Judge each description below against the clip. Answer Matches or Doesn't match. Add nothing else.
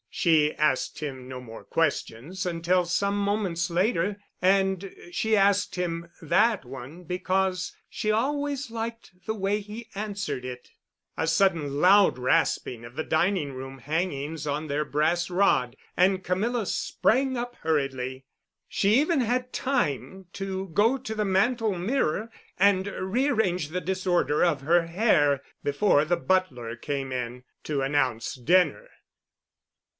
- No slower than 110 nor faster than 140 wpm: Matches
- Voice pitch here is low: Doesn't match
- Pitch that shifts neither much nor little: Doesn't match